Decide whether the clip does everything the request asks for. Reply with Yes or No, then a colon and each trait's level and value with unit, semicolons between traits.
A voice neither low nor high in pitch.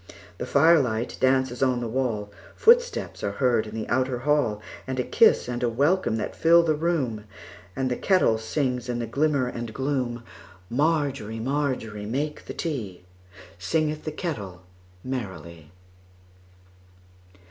No: low, 125 Hz